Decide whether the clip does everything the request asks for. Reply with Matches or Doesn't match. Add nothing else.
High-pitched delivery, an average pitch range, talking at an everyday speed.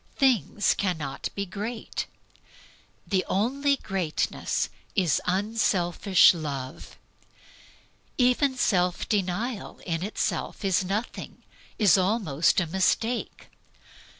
Doesn't match